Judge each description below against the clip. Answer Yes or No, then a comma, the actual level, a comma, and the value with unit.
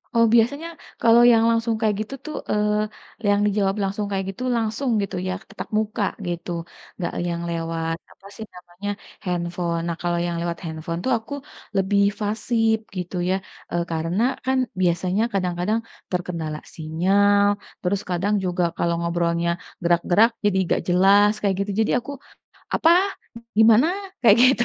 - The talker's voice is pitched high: Yes, high, 195 Hz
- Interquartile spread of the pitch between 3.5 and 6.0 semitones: Yes, average, 3.9 semitones